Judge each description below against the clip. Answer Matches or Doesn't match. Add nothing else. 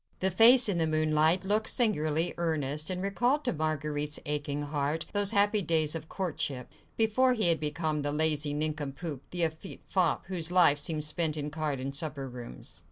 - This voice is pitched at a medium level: Matches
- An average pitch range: Matches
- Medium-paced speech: Matches